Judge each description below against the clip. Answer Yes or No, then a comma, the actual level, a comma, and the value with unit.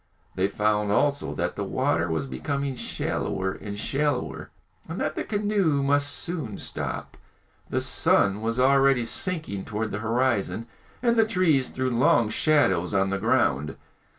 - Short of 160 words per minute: Yes, average, 150 wpm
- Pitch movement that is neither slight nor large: No, wide, 5.9 semitones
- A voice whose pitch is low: Yes, low, 125 Hz